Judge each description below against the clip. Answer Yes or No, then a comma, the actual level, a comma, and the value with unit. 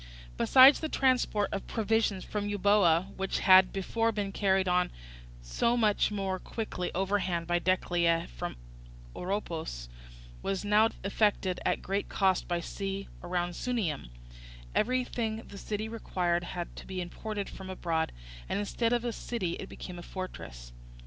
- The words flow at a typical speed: Yes, average, 145 wpm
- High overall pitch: Yes, high, 195 Hz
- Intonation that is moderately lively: Yes, average, 3.3 semitones